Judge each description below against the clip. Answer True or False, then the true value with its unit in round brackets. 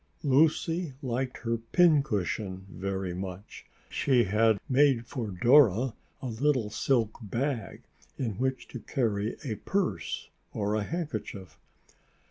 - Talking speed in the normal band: False (115 wpm)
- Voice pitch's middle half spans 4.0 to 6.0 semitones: True (4.8 semitones)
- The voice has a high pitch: False (115 Hz)